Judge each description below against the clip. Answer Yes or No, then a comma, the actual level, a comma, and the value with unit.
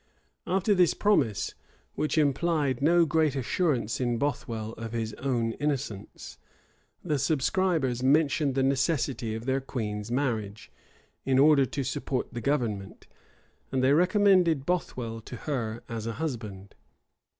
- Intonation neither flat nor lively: Yes, average, 5.0 semitones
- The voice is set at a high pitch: No, low, 135 Hz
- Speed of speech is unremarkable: No, slow, 130 wpm